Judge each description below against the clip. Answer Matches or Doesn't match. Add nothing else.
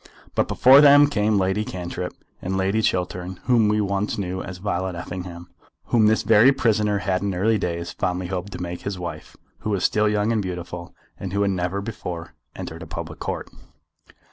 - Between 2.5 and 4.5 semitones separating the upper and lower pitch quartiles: Matches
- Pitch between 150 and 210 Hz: Doesn't match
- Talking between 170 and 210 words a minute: Matches